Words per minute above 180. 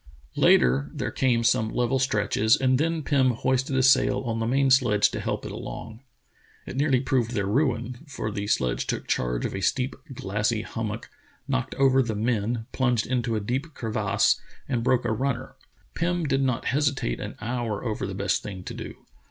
Yes: average, 190 wpm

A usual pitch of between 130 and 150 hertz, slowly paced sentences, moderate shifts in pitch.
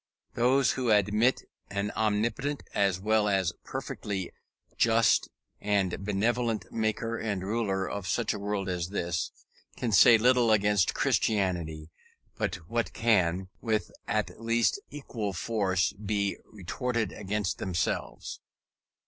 No: low, 105 Hz; slow, 120 wpm; average, 3.0 semitones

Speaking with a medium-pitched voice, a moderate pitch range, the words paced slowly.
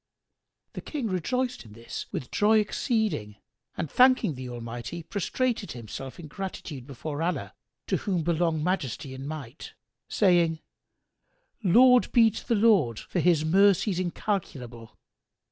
No: medium, 170 Hz; wide, 7.7 semitones; slow, 130 wpm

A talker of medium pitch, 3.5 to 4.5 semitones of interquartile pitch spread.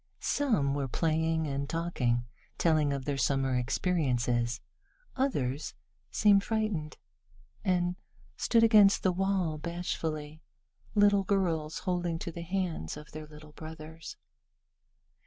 Yes: medium, 160 Hz; average, 4.2 semitones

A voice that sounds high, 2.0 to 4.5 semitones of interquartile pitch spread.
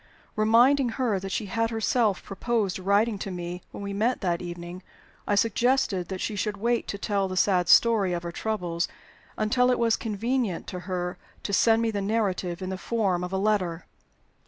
Yes: high, 200 Hz; average, 3.6 semitones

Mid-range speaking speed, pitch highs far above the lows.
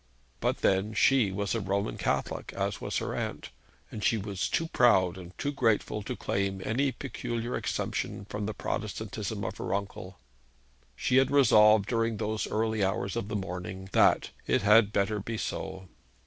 No: average, 170 wpm; average, 2.7 semitones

